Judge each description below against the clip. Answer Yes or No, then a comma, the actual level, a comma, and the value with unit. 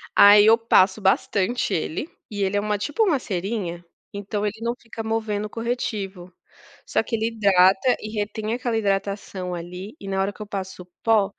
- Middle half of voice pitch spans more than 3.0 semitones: No, average, 2.7 semitones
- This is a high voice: Yes, high, 205 Hz